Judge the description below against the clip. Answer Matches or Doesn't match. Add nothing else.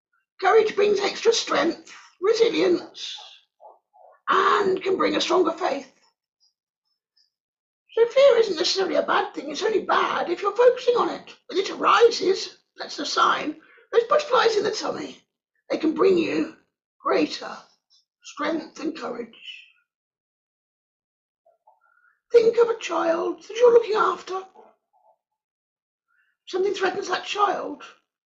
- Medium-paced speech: Doesn't match